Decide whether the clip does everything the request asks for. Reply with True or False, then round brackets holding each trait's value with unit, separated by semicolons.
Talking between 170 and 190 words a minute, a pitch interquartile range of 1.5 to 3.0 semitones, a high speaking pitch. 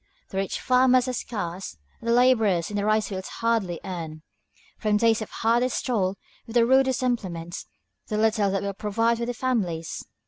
False (180 wpm; 3.8 semitones; 215 Hz)